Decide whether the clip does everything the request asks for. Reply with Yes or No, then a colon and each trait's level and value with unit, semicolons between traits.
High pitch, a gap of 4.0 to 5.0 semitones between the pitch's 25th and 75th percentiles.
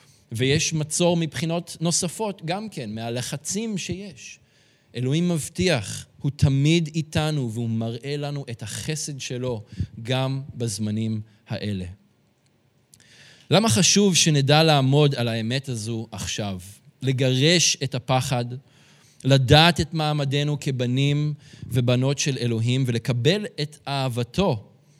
No: medium, 140 Hz; average, 4.4 semitones